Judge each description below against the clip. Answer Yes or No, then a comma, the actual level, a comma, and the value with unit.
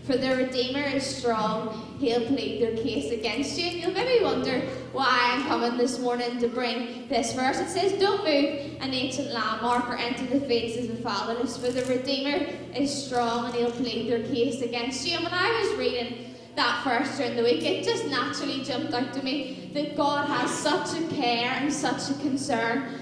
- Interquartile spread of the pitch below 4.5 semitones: Yes, average, 3.1 semitones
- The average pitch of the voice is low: No, very high, 255 Hz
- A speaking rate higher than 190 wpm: Yes, average, 200 wpm